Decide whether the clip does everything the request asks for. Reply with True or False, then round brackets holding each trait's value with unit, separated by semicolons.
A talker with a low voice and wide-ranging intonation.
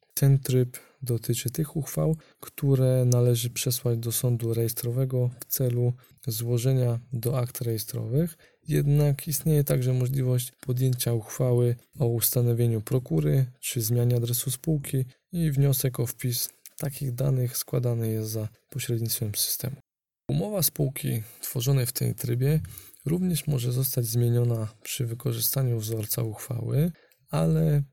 False (125 Hz; 2.7 semitones)